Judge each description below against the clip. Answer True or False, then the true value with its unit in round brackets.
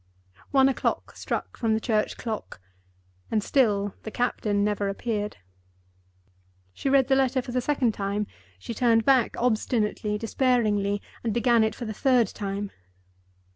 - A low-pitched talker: False (225 Hz)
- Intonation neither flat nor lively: True (3.1 semitones)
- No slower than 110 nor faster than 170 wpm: True (145 wpm)